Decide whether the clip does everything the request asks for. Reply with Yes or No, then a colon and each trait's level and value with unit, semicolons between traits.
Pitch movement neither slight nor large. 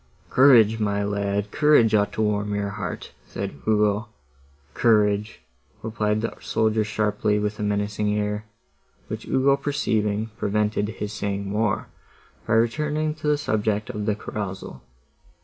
No: narrow, 1.5 semitones